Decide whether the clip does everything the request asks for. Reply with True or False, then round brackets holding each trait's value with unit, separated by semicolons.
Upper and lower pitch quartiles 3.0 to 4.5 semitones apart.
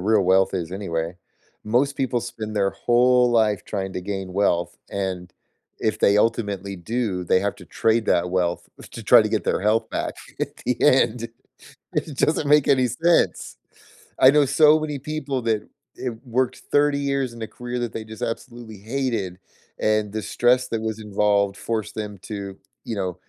True (4.2 semitones)